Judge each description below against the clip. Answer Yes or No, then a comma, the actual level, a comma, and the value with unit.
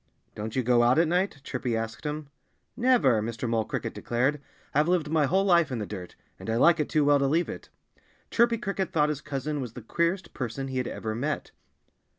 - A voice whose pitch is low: No, medium, 145 Hz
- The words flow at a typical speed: No, fast, 215 wpm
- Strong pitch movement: Yes, wide, 5.9 semitones